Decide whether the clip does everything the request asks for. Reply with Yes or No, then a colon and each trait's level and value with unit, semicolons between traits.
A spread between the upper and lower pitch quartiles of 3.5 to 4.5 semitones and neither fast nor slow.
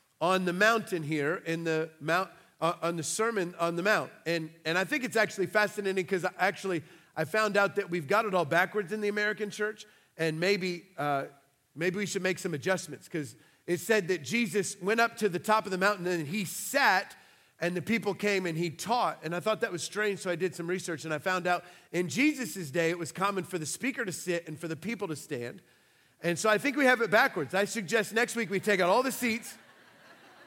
No: average, 3.8 semitones; fast, 230 wpm